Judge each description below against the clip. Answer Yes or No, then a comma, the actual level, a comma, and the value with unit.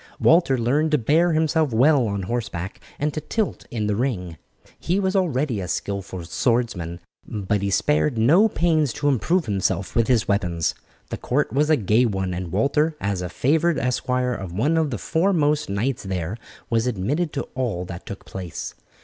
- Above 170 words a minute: Yes, average, 180 wpm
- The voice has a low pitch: Yes, low, 120 Hz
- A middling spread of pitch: No, wide, 7.4 semitones